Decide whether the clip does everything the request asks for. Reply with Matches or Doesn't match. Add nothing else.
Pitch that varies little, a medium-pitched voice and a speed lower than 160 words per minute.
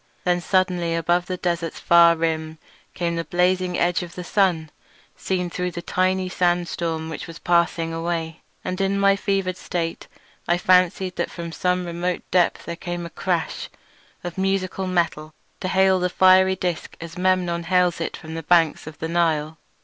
Doesn't match